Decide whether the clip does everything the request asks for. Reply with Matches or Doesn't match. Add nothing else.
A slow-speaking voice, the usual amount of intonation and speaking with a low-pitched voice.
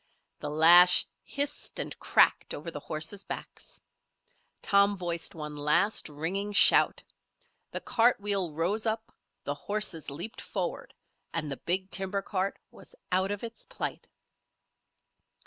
Doesn't match